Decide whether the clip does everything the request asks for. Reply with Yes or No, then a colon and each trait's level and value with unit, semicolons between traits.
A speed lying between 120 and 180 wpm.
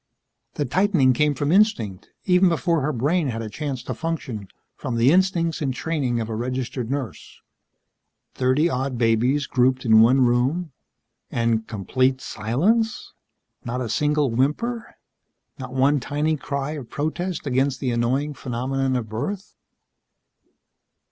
Yes: average, 140 wpm